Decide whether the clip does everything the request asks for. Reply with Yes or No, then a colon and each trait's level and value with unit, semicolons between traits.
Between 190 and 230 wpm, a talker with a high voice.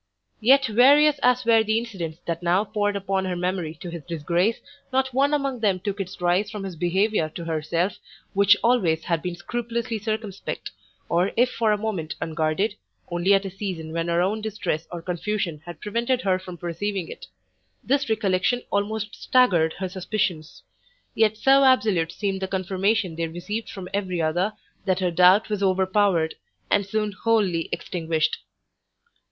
No: average, 165 wpm; high, 195 Hz